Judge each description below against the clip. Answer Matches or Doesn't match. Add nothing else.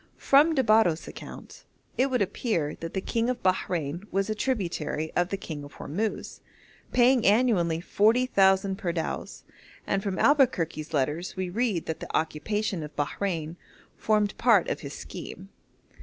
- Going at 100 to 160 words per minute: Matches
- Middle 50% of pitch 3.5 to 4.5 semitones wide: Doesn't match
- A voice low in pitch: Doesn't match